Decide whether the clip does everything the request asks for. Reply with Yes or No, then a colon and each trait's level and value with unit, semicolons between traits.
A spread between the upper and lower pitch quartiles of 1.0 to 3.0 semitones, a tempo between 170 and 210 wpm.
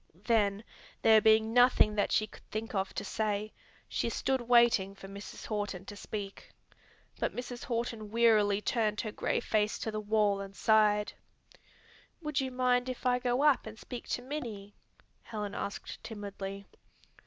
No: average, 2.7 semitones; average, 160 wpm